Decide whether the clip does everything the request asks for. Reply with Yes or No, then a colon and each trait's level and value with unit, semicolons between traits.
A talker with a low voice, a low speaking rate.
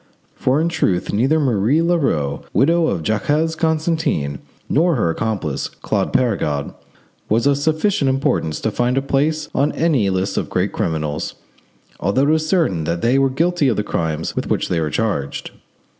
No: low, 130 Hz; average, 170 wpm